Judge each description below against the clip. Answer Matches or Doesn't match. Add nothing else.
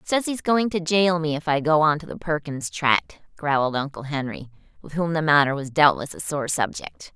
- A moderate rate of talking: Doesn't match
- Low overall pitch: Doesn't match